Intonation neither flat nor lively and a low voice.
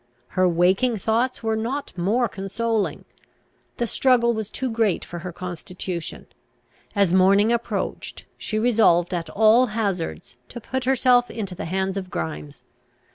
No: average, 4.4 semitones; high, 210 Hz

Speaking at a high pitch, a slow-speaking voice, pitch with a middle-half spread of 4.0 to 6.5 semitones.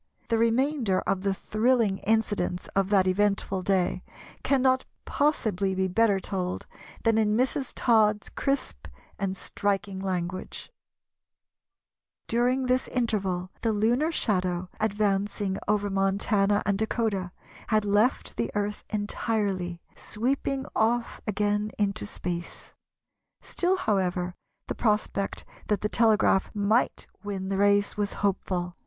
No: high, 205 Hz; slow, 120 wpm; average, 2.8 semitones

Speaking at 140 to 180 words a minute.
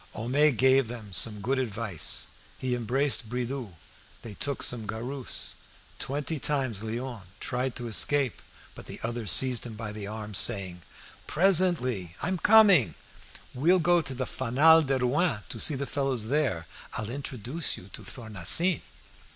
Yes: average, 150 wpm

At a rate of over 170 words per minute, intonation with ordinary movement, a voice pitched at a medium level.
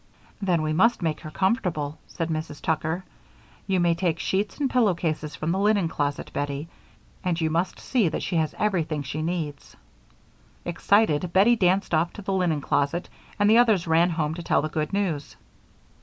Yes: average, 185 wpm; average, 3.6 semitones; medium, 170 Hz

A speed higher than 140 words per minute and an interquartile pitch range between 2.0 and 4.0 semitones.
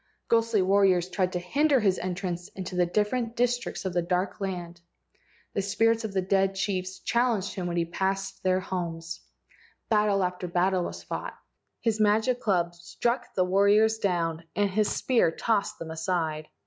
Yes: average, 160 wpm; average, 3.0 semitones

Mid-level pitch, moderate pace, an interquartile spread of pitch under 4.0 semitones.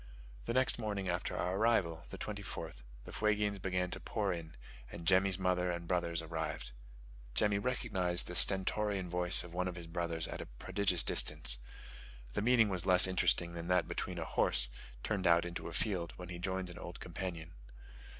No: very low, 90 Hz; average, 180 wpm; narrow, 2.5 semitones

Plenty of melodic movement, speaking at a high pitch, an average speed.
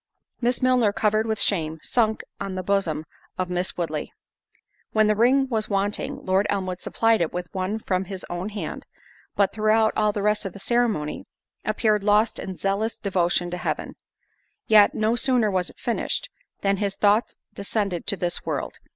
No: average, 2.8 semitones; high, 205 Hz; average, 175 wpm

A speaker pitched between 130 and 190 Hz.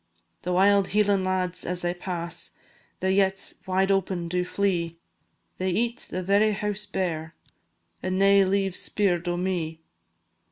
Yes: medium, 185 Hz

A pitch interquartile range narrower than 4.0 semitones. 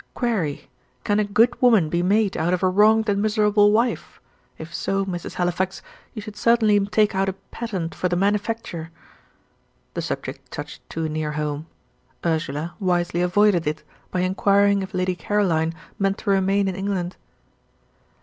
Yes: average, 3.1 semitones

